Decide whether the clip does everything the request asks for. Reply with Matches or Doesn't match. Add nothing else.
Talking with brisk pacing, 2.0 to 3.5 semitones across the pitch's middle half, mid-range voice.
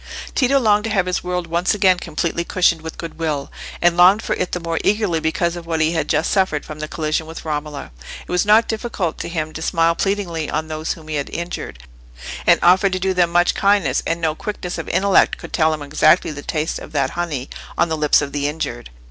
Matches